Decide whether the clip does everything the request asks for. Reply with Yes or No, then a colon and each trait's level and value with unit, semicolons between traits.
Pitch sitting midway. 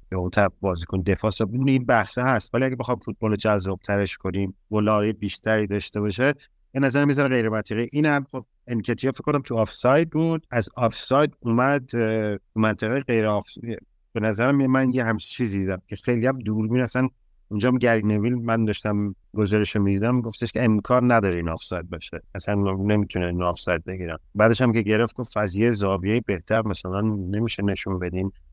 No: low, 110 Hz